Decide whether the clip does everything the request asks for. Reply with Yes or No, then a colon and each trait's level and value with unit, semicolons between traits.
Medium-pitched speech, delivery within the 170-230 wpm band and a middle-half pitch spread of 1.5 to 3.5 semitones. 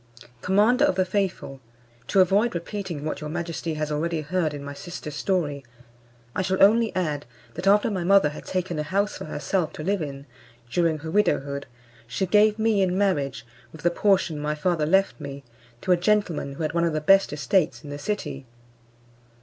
No: medium, 170 Hz; average, 190 wpm; average, 4.5 semitones